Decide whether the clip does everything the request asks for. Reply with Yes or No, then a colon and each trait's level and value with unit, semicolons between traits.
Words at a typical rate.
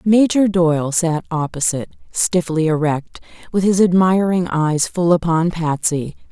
No: slow, 125 wpm